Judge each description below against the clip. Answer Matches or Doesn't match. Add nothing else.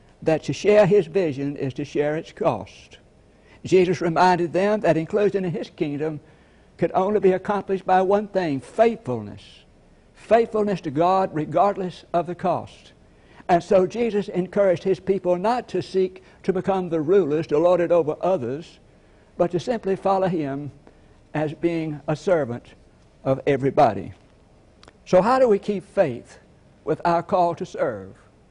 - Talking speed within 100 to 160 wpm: Matches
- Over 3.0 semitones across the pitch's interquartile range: Matches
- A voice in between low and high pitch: Matches